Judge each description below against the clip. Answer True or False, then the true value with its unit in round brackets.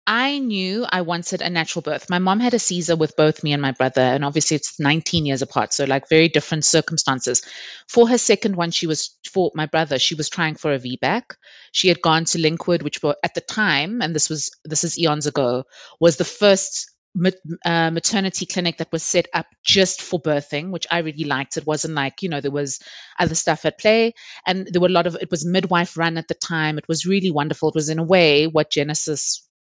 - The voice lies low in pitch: False (165 Hz)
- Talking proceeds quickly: True (230 wpm)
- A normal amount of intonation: True (3.0 semitones)